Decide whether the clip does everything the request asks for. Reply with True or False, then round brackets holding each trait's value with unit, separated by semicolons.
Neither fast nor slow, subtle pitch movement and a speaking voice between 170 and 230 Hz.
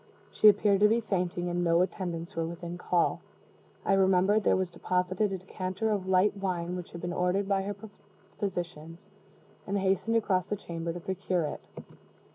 True (175 wpm; 2.1 semitones; 185 Hz)